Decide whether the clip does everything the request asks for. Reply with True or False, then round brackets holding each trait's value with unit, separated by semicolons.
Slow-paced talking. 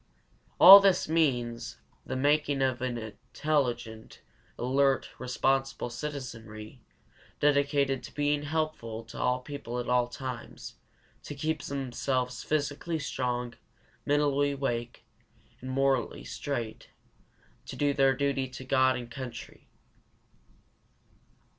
True (105 wpm)